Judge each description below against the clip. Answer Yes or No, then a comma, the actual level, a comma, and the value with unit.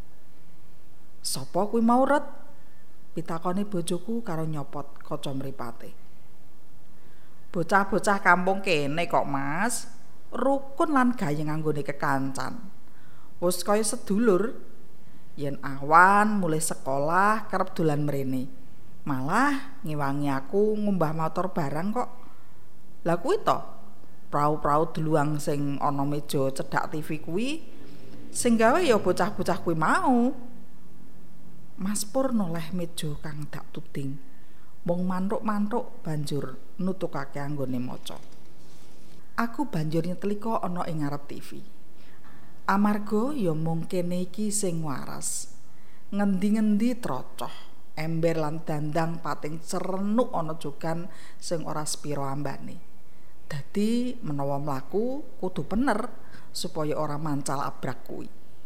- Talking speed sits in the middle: Yes, average, 100 wpm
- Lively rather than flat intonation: Yes, wide, 5.9 semitones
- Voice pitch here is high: No, medium, 170 Hz